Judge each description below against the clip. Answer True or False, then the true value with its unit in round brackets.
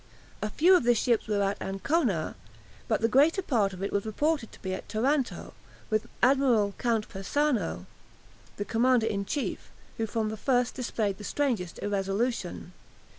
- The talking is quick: False (165 wpm)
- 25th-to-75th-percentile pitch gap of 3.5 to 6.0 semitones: True (4.5 semitones)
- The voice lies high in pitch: True (225 Hz)